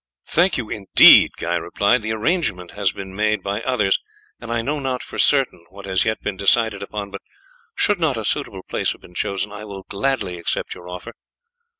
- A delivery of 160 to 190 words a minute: No, average, 200 wpm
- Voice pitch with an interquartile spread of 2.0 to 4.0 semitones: Yes, average, 3.4 semitones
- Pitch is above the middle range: No, low, 105 Hz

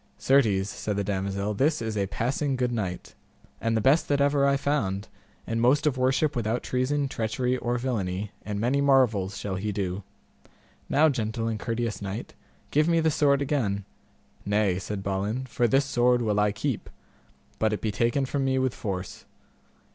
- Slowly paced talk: No, average, 175 wpm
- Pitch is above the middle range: No, low, 115 Hz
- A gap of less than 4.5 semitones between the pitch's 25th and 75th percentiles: No, average, 4.8 semitones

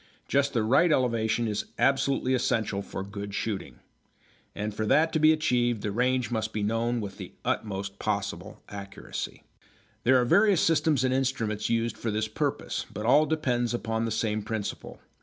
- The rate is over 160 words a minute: Yes, average, 170 wpm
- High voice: No, low, 115 Hz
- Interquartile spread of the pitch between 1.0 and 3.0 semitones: No, average, 3.5 semitones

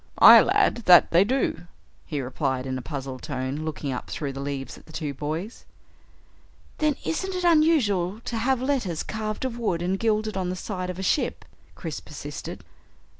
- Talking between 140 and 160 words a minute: No, average, 180 wpm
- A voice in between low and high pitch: Yes, medium, 180 Hz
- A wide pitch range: Yes, wide, 8.1 semitones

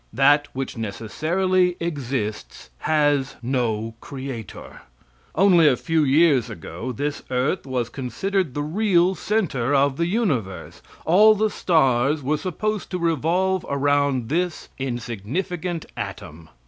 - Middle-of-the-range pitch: Yes, medium, 145 Hz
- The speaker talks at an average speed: No, slow, 120 wpm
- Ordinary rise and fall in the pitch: No, wide, 5.9 semitones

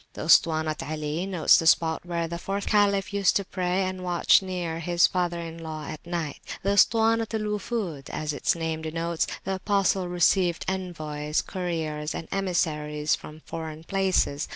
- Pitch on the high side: No, medium, 170 Hz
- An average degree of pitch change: Yes, average, 3.2 semitones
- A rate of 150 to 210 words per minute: Yes, average, 170 wpm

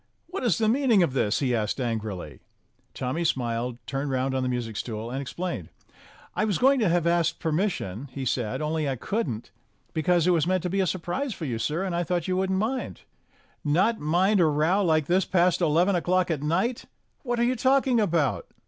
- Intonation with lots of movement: Yes, wide, 6.3 semitones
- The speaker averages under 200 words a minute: No, fast, 205 wpm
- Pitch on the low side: No, medium, 170 Hz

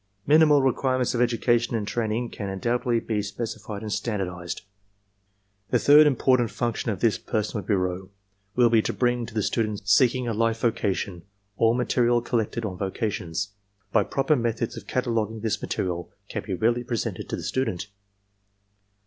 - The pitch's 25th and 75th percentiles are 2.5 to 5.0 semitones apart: Yes, average, 3.0 semitones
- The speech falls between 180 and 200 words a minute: No, average, 165 wpm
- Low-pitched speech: Yes, low, 115 Hz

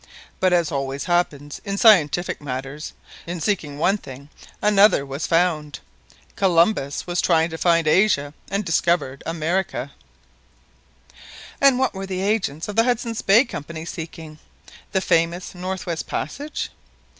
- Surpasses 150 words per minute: No, slow, 135 wpm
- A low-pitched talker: No, medium, 170 Hz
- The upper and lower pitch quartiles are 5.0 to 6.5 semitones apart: No, average, 4.5 semitones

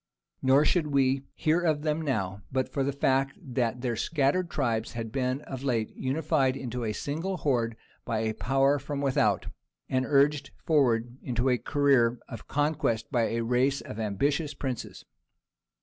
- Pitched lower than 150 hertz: Yes, low, 135 Hz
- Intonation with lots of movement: No, average, 3.3 semitones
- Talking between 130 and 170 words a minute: Yes, average, 165 wpm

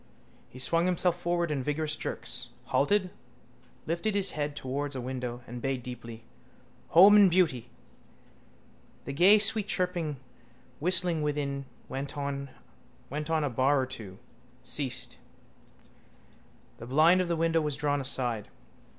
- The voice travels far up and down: No, average, 4.6 semitones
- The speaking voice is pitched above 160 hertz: No, medium, 150 Hz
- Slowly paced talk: Yes, slow, 130 wpm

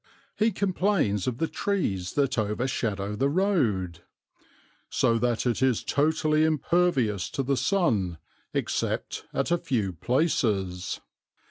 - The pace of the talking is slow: Yes, slow, 120 wpm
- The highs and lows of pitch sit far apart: Yes, wide, 7.8 semitones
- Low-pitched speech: Yes, low, 130 Hz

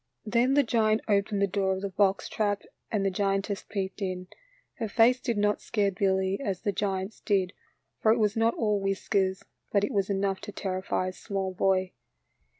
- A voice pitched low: No, high, 200 Hz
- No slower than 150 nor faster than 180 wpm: No, average, 190 wpm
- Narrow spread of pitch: Yes, narrow, 1.8 semitones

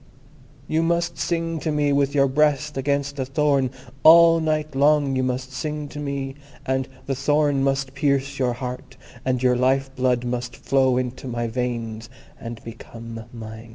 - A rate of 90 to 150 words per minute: No, average, 165 wpm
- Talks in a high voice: No, low, 135 Hz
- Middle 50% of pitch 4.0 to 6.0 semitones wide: No, average, 2.8 semitones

